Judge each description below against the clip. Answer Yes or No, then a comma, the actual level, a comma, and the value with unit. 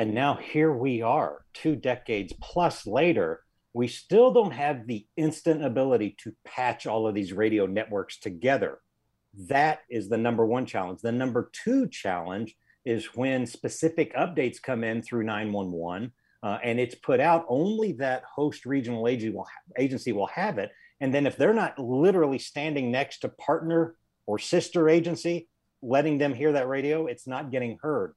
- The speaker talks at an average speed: Yes, average, 170 wpm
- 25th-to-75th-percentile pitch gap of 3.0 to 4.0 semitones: No, average, 5.1 semitones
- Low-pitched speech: Yes, low, 130 Hz